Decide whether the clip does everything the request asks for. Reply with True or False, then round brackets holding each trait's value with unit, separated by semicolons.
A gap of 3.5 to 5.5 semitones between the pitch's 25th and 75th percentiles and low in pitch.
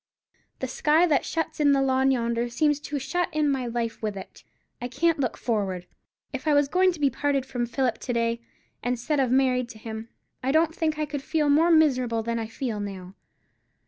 False (4.2 semitones; 260 Hz)